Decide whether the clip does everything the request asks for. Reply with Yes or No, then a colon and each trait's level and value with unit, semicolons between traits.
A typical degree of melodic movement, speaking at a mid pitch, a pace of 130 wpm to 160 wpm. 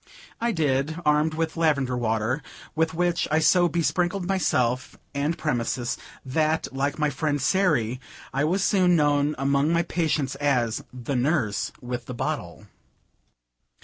Yes: average, 4.2 semitones; medium, 150 Hz; average, 140 wpm